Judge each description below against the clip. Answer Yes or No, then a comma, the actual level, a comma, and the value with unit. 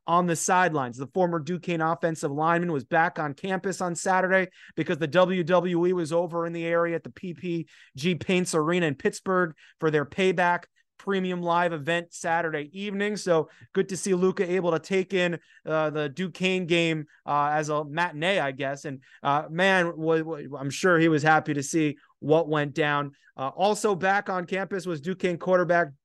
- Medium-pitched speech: Yes, medium, 170 Hz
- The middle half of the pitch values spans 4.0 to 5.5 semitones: No, average, 2.8 semitones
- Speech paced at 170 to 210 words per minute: Yes, average, 175 wpm